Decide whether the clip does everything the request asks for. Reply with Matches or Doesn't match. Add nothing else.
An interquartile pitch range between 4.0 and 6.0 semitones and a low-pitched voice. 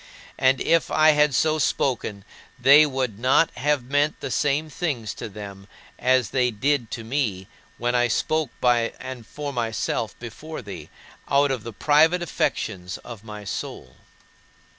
Matches